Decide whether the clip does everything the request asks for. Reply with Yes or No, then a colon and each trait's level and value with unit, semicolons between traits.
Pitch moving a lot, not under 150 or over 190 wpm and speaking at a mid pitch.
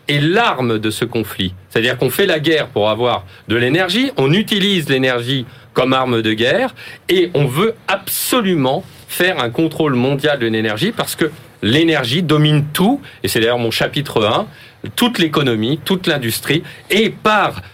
Yes: wide, 7.0 semitones; average, 160 wpm; medium, 145 Hz